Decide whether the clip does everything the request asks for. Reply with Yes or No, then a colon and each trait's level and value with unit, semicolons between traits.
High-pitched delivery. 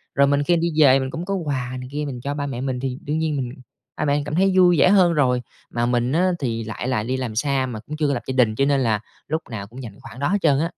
No: low, 135 Hz